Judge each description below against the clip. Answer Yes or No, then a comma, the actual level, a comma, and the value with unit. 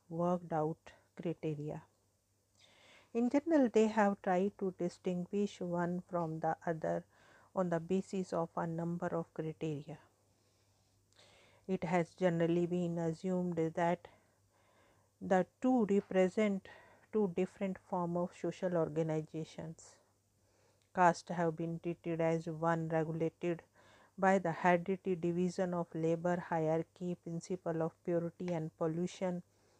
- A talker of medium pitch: Yes, medium, 170 Hz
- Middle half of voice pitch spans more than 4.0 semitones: No, narrow, 2.5 semitones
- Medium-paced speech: No, slow, 115 wpm